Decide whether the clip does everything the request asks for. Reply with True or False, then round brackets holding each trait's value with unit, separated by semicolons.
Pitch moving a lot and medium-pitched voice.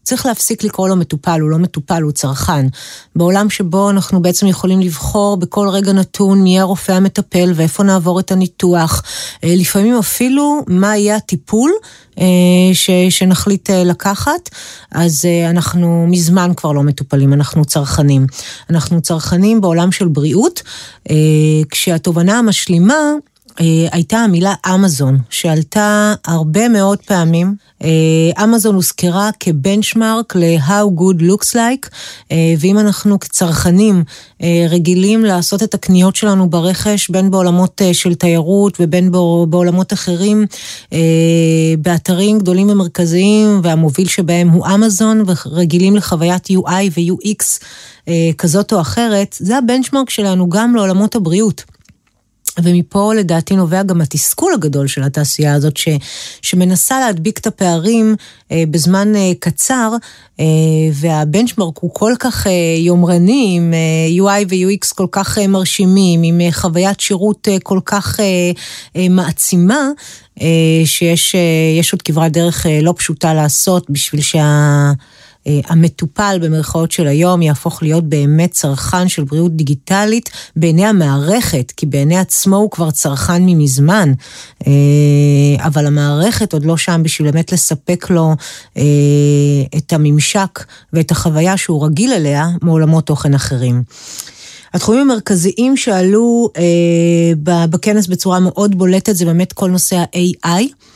False (3.5 semitones; 180 Hz)